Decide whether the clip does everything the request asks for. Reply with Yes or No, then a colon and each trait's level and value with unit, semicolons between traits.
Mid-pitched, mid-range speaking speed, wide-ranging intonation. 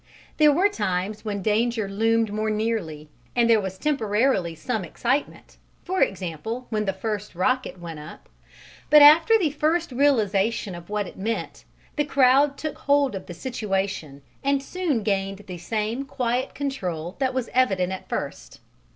No: high, 220 Hz; average, 160 wpm; wide, 5.9 semitones